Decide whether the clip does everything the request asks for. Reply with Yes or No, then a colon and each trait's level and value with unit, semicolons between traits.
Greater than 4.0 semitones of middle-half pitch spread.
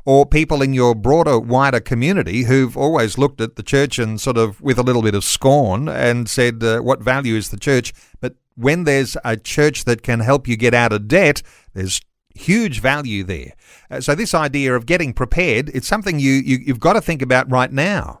No: average, 3.4 semitones